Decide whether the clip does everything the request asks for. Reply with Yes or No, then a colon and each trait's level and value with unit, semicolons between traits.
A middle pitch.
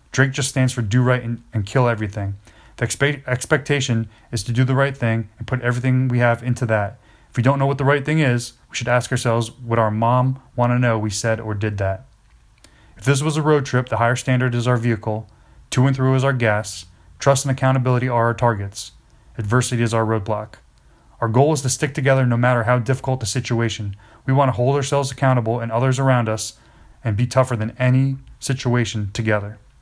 No: low, 120 Hz